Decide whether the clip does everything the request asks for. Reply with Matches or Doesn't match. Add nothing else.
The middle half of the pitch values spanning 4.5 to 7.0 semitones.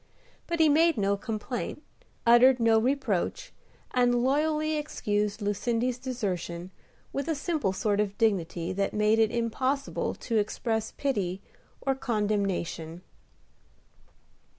Matches